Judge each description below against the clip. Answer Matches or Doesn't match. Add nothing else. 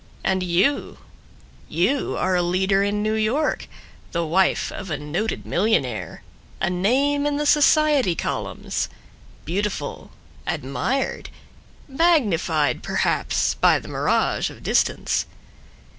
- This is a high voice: Matches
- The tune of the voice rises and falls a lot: Matches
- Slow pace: Matches